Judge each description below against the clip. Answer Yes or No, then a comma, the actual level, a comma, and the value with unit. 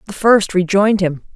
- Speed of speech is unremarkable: Yes, average, 175 wpm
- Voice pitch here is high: Yes, high, 195 Hz